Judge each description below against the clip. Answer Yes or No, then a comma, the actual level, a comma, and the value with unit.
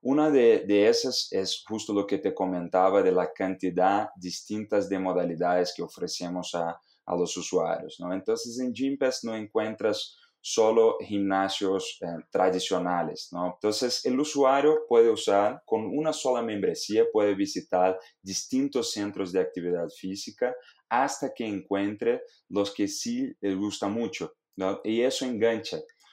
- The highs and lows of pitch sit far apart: Yes, wide, 8.6 semitones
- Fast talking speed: No, average, 140 wpm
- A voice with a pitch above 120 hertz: No, low, 105 Hz